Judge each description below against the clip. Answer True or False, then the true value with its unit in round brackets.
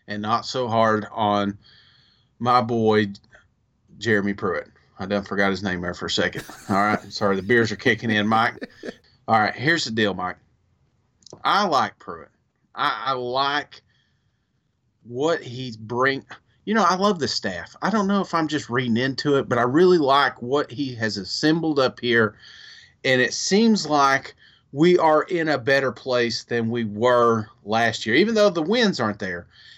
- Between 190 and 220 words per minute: False (175 wpm)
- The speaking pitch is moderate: False (120 Hz)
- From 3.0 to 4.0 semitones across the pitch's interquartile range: False (4.4 semitones)